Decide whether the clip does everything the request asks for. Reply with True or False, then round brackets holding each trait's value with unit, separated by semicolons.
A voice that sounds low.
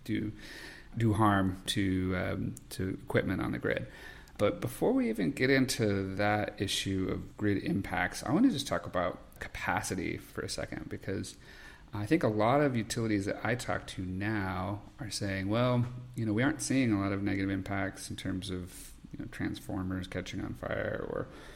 True (105 Hz)